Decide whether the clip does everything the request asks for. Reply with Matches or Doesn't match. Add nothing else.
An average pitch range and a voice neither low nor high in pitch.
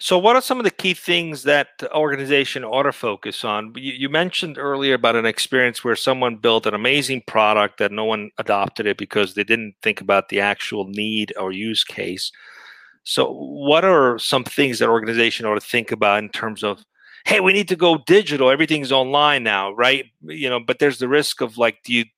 Doesn't match